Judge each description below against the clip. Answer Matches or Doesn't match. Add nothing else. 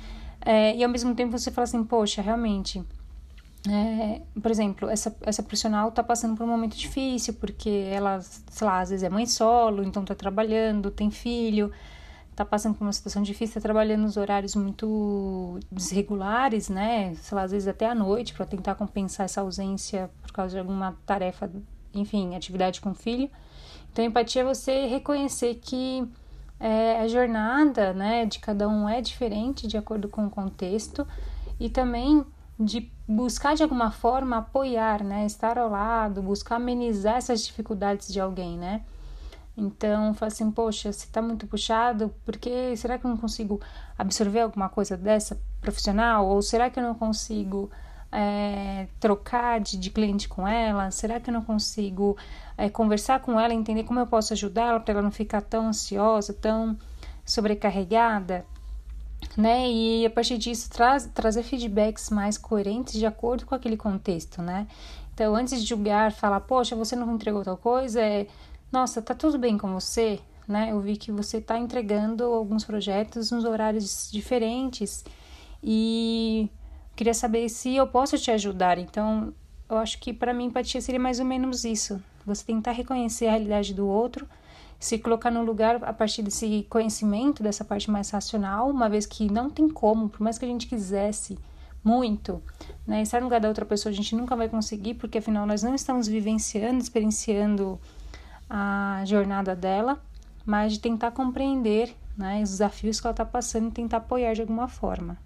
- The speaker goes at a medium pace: Matches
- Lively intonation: Doesn't match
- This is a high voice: Matches